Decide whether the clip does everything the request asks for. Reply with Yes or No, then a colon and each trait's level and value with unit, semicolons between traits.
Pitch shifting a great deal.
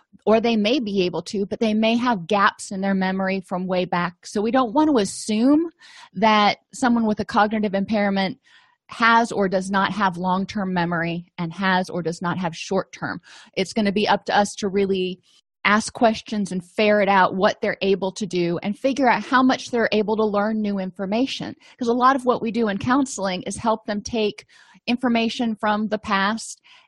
No: average, 3.2 semitones